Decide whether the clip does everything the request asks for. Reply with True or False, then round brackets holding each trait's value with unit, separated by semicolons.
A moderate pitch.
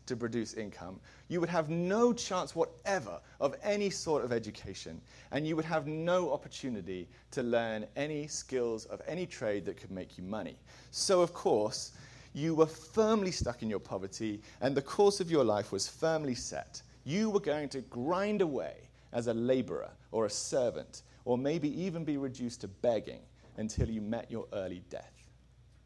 False (130 Hz)